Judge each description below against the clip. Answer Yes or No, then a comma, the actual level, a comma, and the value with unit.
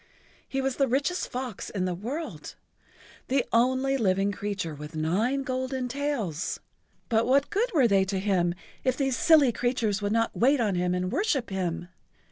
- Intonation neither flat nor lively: No, wide, 5.8 semitones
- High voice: Yes, high, 235 Hz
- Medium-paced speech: Yes, average, 160 wpm